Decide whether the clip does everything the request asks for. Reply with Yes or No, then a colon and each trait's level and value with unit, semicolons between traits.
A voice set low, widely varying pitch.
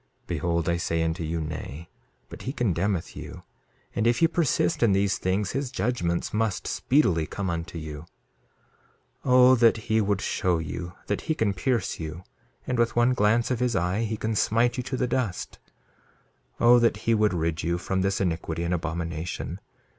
Yes: low, 100 Hz; wide, 5.7 semitones